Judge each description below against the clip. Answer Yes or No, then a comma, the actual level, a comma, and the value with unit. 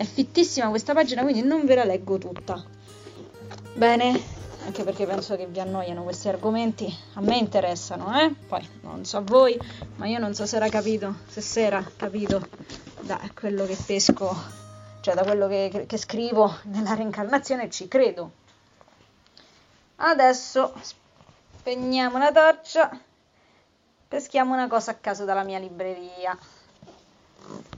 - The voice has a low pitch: No, high, 210 Hz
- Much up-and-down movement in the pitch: No, average, 4.7 semitones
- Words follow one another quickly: No, average, 140 wpm